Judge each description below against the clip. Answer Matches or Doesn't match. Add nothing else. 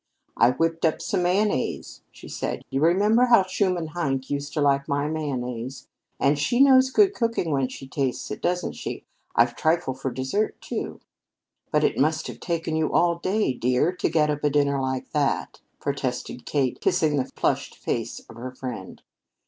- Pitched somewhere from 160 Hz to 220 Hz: Doesn't match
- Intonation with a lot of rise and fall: Doesn't match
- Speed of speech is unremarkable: Matches